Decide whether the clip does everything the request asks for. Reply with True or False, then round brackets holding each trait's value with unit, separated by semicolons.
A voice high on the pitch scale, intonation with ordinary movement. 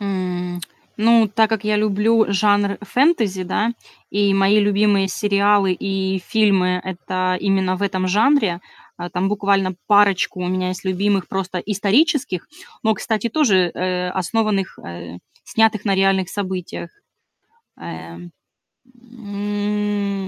False (195 Hz; 2.1 semitones)